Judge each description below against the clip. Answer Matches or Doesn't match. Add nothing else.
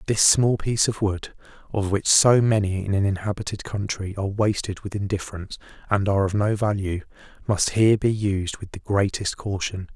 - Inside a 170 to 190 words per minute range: Matches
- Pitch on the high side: Doesn't match